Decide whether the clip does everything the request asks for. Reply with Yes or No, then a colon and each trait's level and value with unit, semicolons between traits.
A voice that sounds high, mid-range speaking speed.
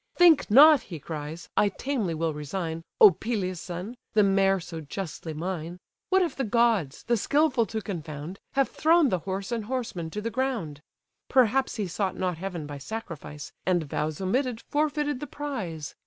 Yes: high, 195 Hz; average, 170 wpm